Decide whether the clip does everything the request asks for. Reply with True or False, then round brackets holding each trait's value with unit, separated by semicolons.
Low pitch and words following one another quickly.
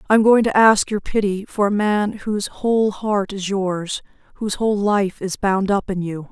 False (200 Hz; 220 wpm)